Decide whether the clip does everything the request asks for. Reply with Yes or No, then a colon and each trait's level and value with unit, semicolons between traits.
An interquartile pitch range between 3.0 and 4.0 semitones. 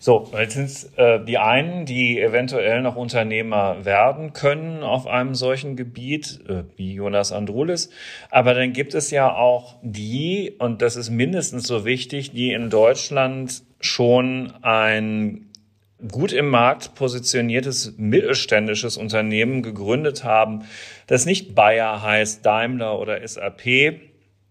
Yes: average, 3.3 semitones